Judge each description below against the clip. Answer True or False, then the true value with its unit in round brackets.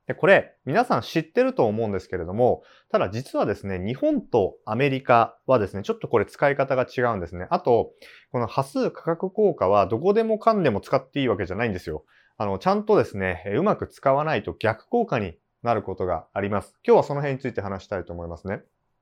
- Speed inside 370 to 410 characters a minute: False (430 characters per minute)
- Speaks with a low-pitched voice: True (125 Hz)